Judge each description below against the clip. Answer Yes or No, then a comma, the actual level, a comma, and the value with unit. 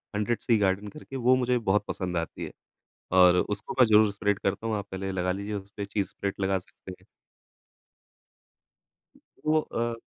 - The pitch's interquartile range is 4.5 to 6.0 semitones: No, average, 2.9 semitones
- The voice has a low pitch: Yes, low, 100 Hz